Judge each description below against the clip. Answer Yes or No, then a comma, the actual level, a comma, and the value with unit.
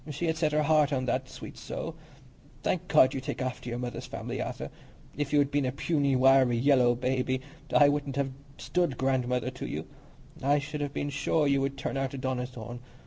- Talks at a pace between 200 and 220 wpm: Yes, fast, 205 wpm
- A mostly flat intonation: Yes, narrow, 2.1 semitones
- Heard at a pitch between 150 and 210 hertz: No, low, 135 Hz